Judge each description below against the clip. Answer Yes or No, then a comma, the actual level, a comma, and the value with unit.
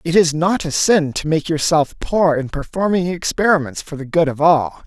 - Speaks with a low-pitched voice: No, medium, 165 Hz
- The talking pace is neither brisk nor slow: No, fast, 210 wpm